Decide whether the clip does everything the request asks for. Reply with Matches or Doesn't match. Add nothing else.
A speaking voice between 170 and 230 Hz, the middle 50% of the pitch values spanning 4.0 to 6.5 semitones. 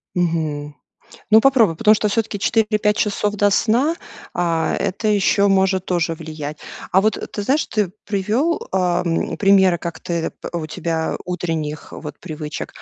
Matches